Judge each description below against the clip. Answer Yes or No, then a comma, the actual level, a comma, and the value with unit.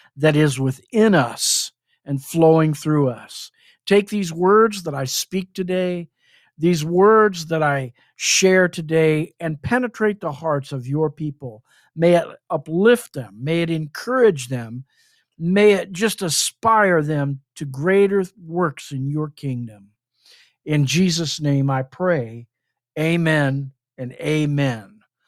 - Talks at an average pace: No, slow, 130 wpm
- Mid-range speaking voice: Yes, medium, 155 Hz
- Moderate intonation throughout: Yes, average, 4.9 semitones